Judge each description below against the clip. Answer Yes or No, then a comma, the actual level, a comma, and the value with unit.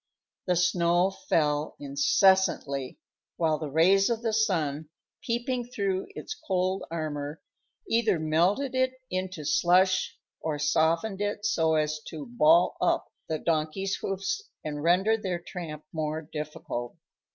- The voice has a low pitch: No, medium, 175 Hz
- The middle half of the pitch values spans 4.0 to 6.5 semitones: Yes, average, 4.3 semitones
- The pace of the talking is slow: Yes, slow, 130 wpm